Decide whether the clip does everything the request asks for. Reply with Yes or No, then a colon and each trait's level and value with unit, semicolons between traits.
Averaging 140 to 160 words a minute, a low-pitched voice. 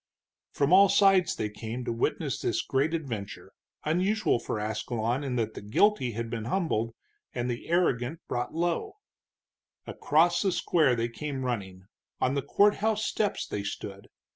Yes: average, 155 wpm; low, 130 Hz